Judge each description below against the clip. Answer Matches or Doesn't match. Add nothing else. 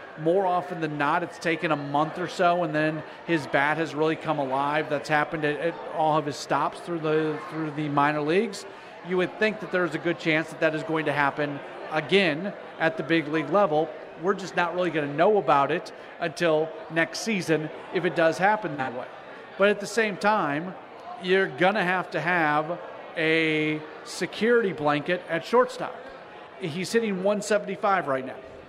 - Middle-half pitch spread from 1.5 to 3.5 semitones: Matches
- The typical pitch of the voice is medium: Matches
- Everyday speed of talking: Matches